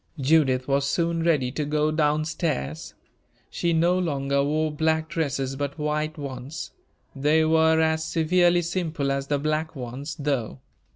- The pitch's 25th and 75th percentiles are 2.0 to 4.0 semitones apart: Yes, narrow, 2.5 semitones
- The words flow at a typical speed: Yes, average, 150 wpm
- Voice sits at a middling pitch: Yes, medium, 150 Hz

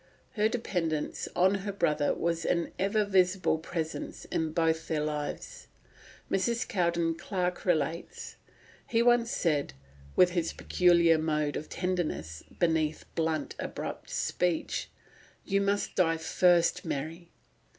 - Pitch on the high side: No, medium, 170 Hz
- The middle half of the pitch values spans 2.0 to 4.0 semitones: Yes, average, 2.8 semitones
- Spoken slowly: Yes, slow, 120 wpm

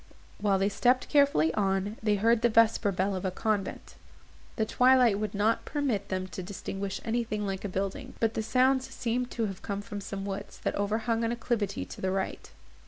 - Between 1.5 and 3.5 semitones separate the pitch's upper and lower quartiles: Yes, average, 2.9 semitones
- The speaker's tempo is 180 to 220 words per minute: Yes, average, 190 wpm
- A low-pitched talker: No, high, 210 Hz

